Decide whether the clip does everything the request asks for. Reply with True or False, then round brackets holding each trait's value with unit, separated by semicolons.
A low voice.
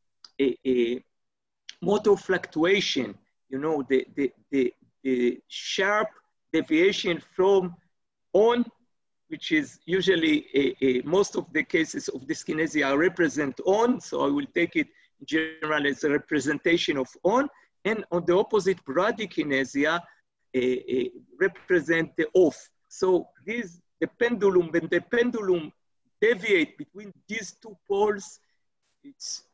False (185 Hz)